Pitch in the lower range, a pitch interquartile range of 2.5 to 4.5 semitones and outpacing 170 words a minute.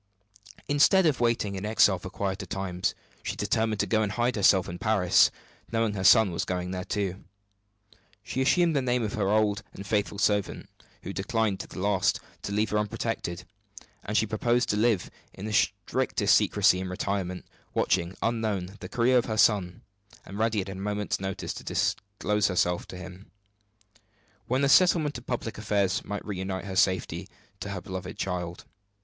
Yes: low, 100 Hz; average, 3.0 semitones; average, 180 wpm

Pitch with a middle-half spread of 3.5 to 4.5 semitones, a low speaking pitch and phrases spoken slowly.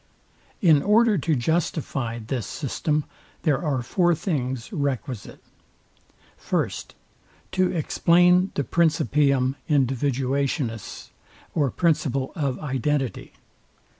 No: average, 4.2 semitones; medium, 145 Hz; slow, 90 wpm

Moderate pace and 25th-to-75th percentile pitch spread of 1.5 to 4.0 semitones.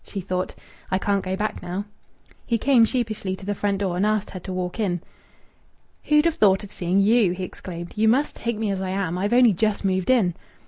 No: fast, 225 wpm; average, 2.9 semitones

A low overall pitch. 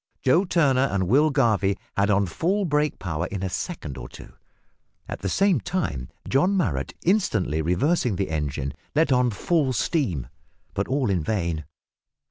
Yes: low, 110 Hz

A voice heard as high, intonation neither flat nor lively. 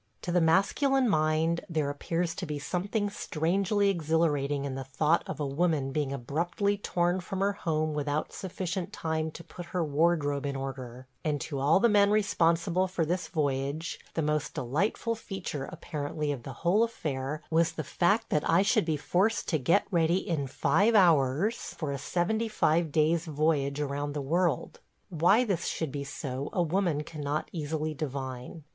No: medium, 160 Hz; average, 4.0 semitones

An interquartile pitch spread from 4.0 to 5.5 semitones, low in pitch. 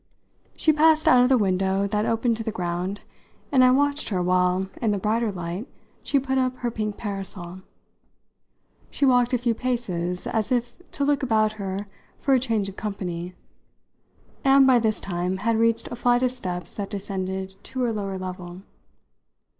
No: average, 4.8 semitones; high, 215 Hz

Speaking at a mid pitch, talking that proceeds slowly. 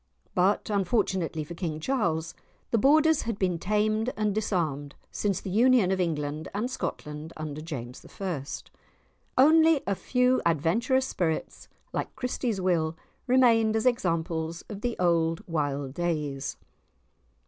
Yes: medium, 180 Hz; slow, 130 wpm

